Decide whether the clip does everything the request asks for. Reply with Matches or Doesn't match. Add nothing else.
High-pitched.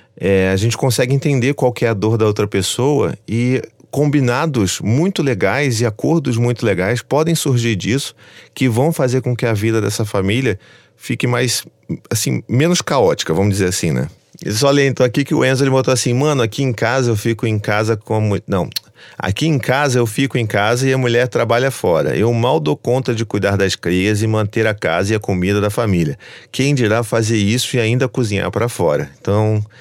Doesn't match